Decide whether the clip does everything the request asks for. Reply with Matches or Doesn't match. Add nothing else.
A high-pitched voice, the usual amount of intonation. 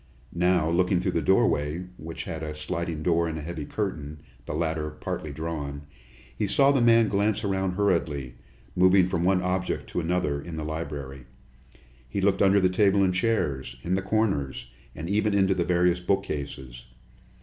Doesn't match